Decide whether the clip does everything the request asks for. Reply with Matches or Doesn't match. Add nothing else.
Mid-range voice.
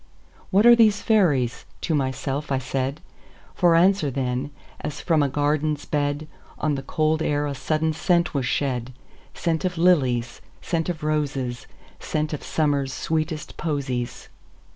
Matches